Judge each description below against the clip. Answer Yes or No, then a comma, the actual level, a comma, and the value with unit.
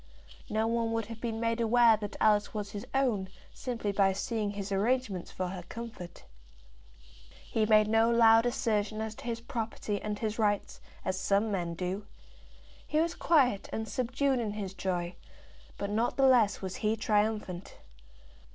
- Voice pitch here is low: No, high, 215 Hz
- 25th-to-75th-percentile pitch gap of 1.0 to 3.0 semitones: Yes, narrow, 2.4 semitones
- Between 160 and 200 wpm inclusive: Yes, average, 165 wpm